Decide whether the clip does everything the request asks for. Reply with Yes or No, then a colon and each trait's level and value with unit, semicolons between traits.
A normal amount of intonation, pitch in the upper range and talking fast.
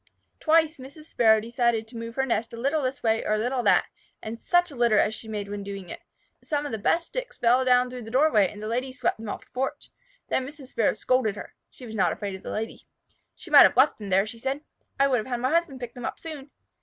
Yes: average, 3.7 semitones; high, 245 Hz; fast, 265 wpm